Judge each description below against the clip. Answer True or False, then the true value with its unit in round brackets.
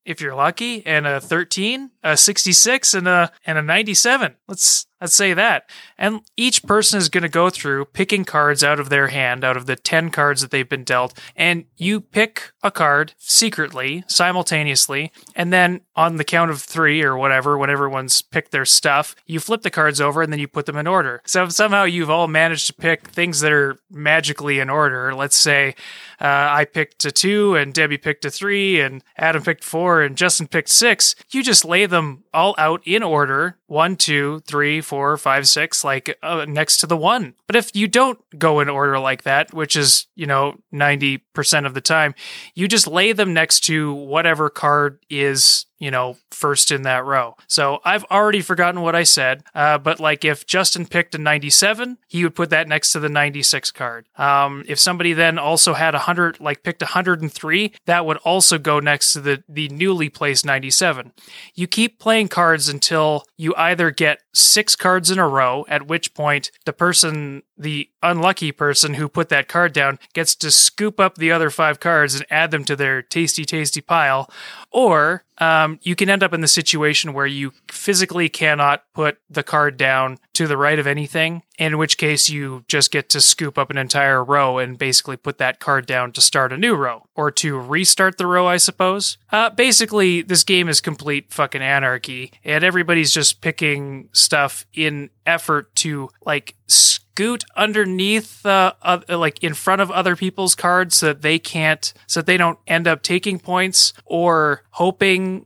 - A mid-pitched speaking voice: True (155 Hz)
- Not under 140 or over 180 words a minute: False (195 wpm)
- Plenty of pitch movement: False (3.8 semitones)